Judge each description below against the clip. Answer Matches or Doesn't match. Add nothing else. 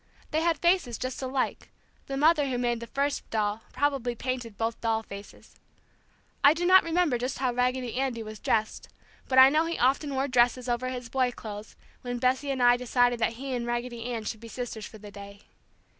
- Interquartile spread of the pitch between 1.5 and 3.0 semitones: Matches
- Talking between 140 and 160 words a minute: Doesn't match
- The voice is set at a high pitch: Matches